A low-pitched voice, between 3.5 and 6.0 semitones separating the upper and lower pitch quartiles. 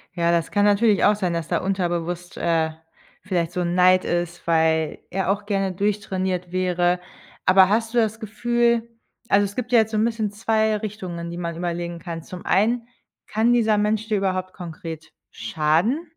No: high, 190 Hz; average, 3.9 semitones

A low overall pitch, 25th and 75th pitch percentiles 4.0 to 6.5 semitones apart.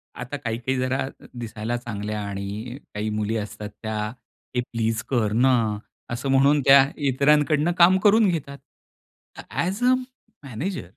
Yes: low, 125 Hz; average, 4.5 semitones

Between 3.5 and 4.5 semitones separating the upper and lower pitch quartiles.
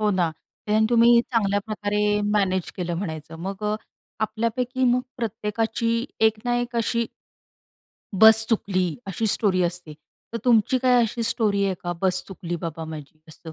Yes: average, 3.8 semitones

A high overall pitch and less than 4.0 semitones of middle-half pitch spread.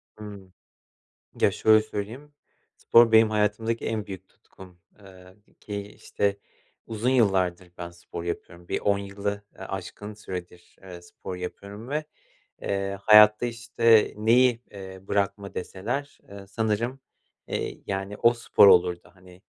No: low, 100 Hz; average, 2.9 semitones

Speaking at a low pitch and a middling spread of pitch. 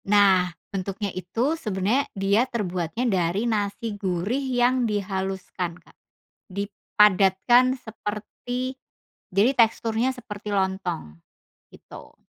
No: high, 205 Hz; average, 3.8 semitones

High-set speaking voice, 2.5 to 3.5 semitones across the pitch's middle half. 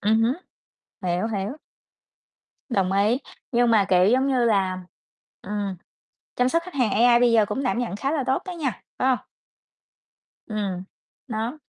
No: high, 230 Hz; average, 4.3 semitones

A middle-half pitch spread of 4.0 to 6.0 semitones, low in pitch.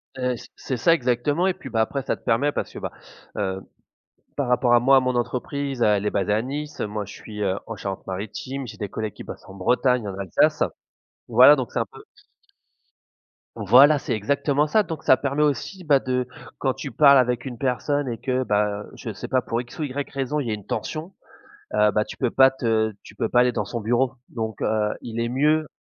Yes: average, 4.3 semitones; low, 125 Hz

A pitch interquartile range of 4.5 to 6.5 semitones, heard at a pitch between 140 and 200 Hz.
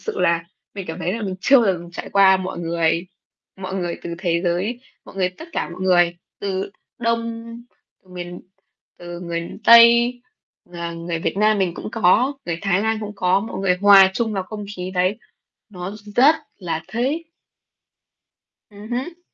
No: average, 4.0 semitones; high, 190 Hz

